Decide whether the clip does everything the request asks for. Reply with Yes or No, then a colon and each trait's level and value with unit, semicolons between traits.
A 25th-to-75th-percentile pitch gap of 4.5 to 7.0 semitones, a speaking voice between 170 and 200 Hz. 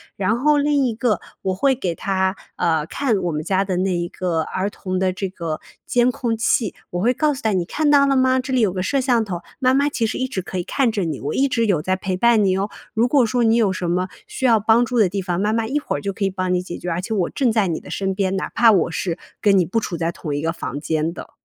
Yes: average, 4.8 semitones; high, 195 Hz